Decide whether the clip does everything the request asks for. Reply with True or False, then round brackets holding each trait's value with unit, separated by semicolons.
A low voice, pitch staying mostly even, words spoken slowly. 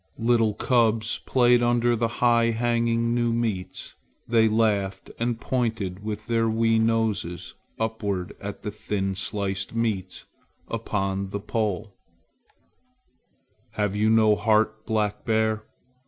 True (110 Hz; 2.1 semitones; 120 wpm)